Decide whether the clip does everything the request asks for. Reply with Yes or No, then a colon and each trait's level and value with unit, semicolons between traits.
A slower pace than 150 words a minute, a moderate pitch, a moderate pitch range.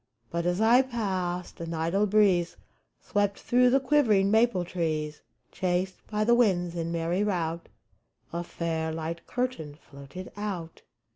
Yes: average, 140 wpm; medium, 180 Hz; average, 4.0 semitones